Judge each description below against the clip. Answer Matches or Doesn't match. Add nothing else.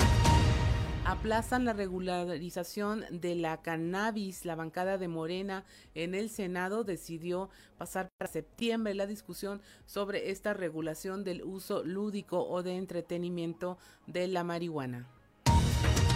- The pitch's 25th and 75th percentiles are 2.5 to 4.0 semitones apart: Matches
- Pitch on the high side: Doesn't match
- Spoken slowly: Matches